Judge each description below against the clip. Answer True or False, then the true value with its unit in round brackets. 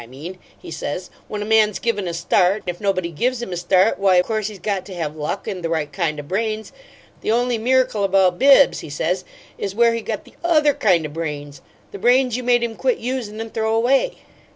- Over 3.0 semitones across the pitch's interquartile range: True (5.0 semitones)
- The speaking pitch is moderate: False (205 Hz)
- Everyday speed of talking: False (225 wpm)